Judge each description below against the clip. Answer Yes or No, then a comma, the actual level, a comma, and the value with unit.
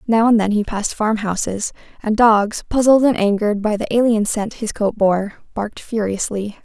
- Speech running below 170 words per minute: No, average, 180 wpm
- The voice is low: No, high, 215 Hz